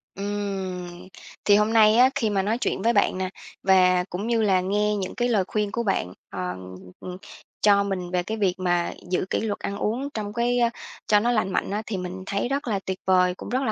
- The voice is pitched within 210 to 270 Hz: No, high, 200 Hz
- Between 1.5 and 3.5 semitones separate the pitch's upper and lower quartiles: Yes, average, 3.0 semitones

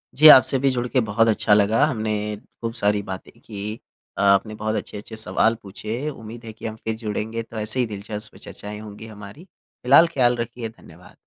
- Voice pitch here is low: Yes, low, 110 Hz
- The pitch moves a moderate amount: No, narrow, 2.2 semitones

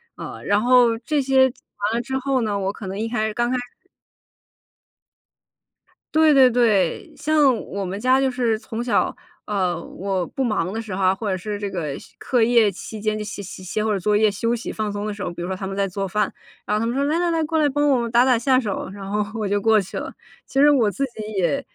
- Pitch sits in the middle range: No, high, 220 Hz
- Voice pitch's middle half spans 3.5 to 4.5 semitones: Yes, average, 4.1 semitones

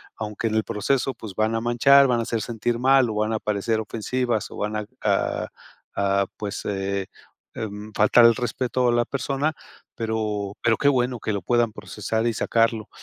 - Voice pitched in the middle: No, low, 110 Hz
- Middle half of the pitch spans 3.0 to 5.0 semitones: No, narrow, 2.4 semitones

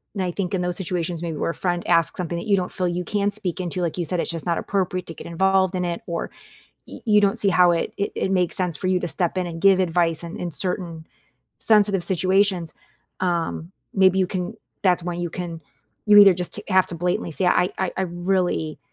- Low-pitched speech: No, medium, 180 Hz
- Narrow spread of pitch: Yes, narrow, 1.8 semitones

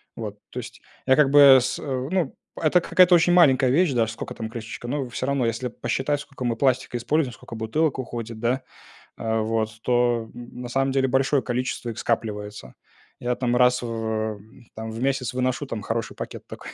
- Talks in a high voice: No, low, 125 Hz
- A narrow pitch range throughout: No, average, 3.0 semitones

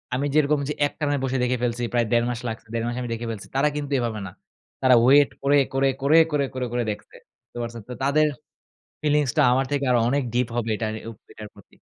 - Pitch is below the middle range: Yes, low, 130 Hz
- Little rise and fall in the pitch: No, average, 3.2 semitones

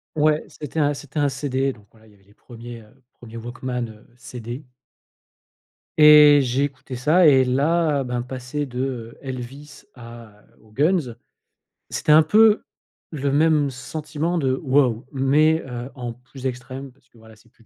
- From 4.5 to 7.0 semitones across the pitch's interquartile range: No, average, 3.5 semitones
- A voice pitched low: Yes, low, 130 Hz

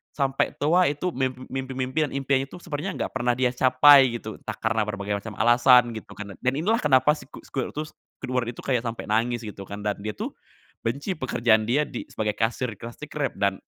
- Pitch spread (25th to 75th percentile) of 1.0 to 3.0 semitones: No, average, 3.8 semitones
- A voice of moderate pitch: No, low, 125 Hz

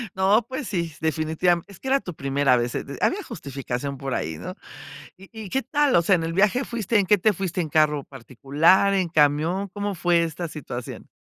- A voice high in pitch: No, medium, 170 Hz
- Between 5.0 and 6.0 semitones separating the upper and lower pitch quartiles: Yes, wide, 5.5 semitones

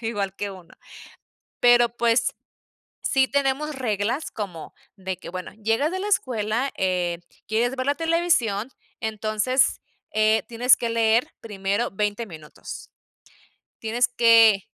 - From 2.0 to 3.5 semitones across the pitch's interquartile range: No, average, 3.9 semitones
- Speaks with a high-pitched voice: Yes, high, 225 Hz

